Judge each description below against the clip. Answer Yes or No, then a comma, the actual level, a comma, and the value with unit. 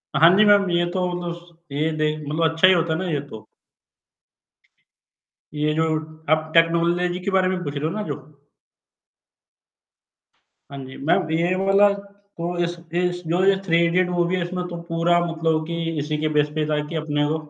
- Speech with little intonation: Yes, narrow, 2.3 semitones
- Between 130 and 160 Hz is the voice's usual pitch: No, medium, 170 Hz